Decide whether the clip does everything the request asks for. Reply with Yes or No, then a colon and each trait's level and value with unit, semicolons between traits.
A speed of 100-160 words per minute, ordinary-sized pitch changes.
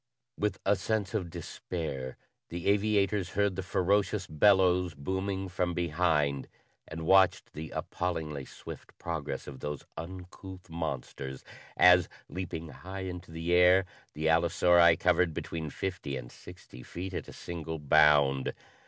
Yes: slow, 135 wpm; average, 3.3 semitones